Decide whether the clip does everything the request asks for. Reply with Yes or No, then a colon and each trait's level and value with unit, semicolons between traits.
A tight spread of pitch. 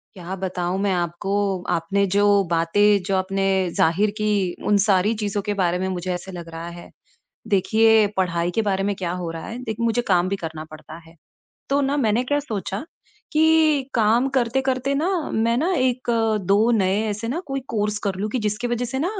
No: average, 4.3 semitones